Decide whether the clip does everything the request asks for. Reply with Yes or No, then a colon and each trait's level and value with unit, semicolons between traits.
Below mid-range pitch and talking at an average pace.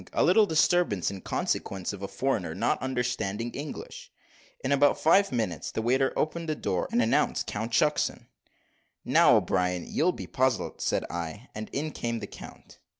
Yes: low, 120 Hz; average, 165 wpm